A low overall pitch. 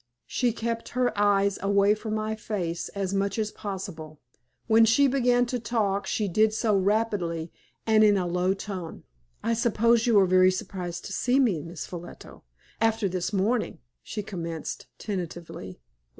No: high, 205 Hz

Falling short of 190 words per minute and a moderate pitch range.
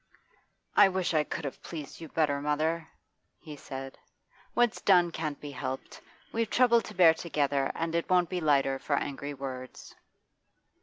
Yes: average, 160 wpm; average, 3.6 semitones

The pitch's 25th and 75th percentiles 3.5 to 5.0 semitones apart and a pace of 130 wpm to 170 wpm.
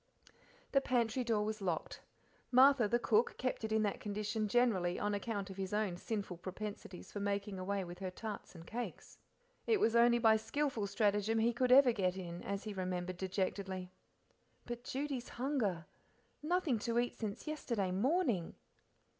Yes: average, 4.0 semitones; average, 165 wpm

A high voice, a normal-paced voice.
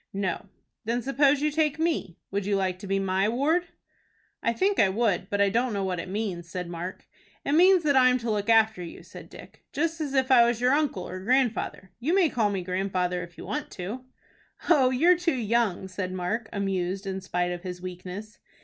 No: high, 210 Hz; fast, 215 wpm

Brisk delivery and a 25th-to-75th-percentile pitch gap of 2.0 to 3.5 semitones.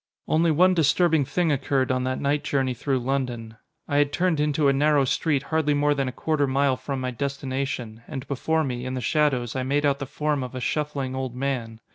Yes: fast, 215 wpm; narrow, 2.4 semitones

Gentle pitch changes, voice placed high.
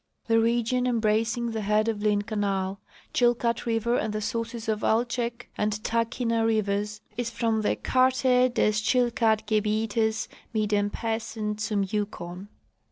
Yes: narrow, 1.8 semitones; high, 220 Hz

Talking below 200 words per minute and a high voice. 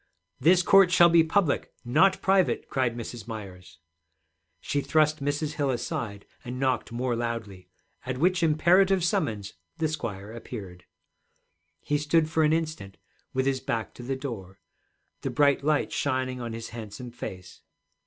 No: average, 150 wpm; low, 130 Hz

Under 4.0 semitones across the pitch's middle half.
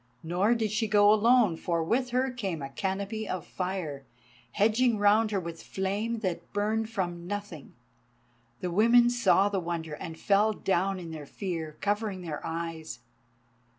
No: average, 4.3 semitones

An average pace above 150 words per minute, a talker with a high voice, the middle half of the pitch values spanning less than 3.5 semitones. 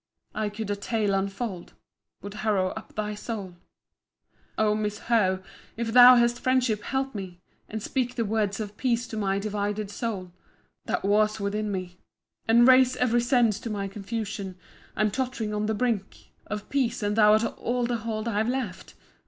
Yes: average, 175 wpm; high, 215 Hz; narrow, 2.6 semitones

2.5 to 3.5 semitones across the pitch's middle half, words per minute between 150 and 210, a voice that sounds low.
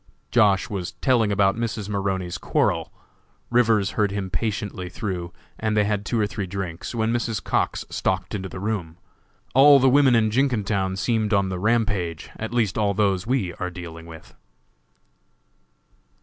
Yes: average, 3.1 semitones; average, 160 wpm; low, 105 Hz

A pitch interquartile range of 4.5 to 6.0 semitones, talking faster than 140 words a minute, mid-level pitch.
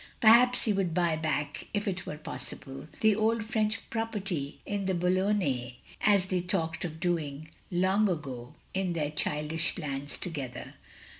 Yes: average, 5.1 semitones; average, 155 wpm; medium, 175 Hz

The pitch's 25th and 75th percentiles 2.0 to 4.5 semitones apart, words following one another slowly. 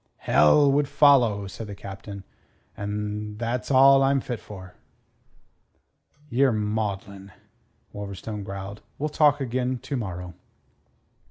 No: average, 5.0 semitones; slow, 110 wpm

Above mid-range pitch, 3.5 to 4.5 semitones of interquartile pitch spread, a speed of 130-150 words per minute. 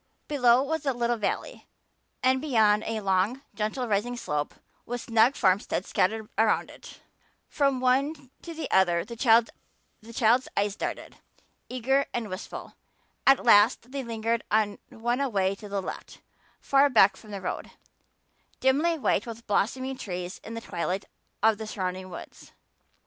Yes: high, 230 Hz; average, 4.0 semitones; average, 145 wpm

